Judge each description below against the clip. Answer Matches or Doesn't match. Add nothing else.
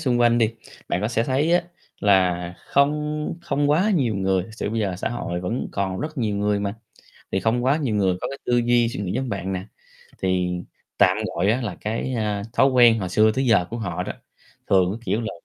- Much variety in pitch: Doesn't match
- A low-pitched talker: Matches